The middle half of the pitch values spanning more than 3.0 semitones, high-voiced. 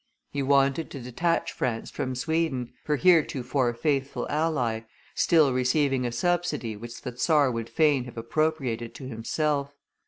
No: average, 4.0 semitones; low, 135 Hz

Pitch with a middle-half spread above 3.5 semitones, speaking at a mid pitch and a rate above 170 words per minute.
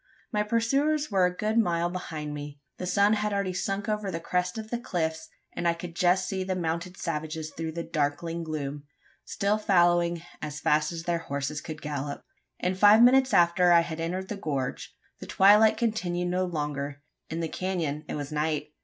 Yes: average, 4.0 semitones; medium, 175 Hz; average, 190 wpm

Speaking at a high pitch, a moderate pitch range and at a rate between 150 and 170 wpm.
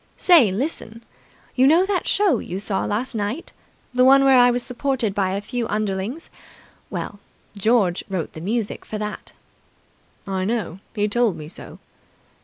Yes: high, 225 Hz; average, 4.2 semitones; average, 160 wpm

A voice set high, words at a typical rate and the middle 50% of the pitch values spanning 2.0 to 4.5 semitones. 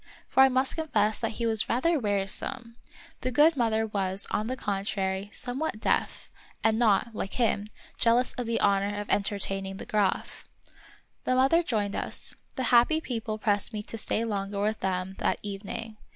Yes: high, 220 Hz; average, 175 wpm; average, 3.5 semitones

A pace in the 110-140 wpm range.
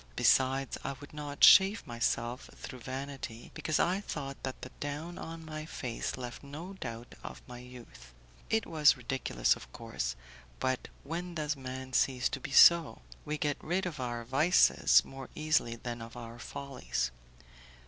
No: average, 160 wpm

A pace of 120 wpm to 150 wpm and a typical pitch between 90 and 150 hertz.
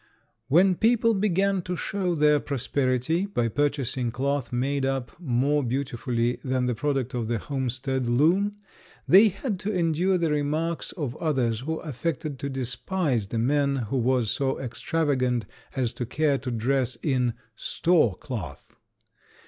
Yes: average, 145 wpm; low, 135 Hz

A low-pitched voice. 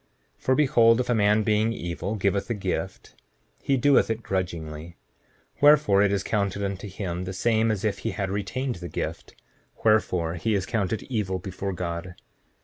Yes: low, 100 Hz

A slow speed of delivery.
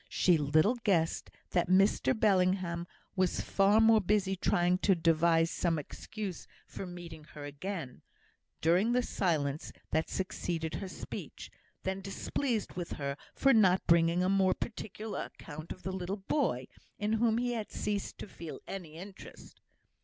No: average, 150 wpm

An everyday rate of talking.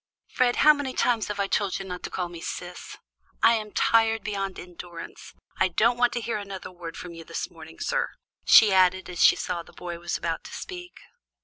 No: fast, 215 wpm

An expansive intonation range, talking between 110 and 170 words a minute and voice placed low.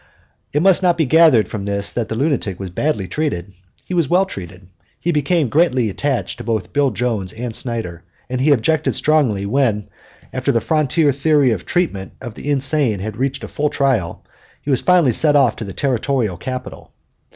No: wide, 5.9 semitones; average, 190 wpm; low, 130 Hz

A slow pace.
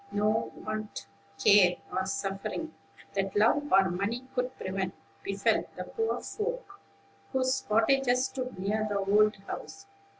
Yes: slow, 130 wpm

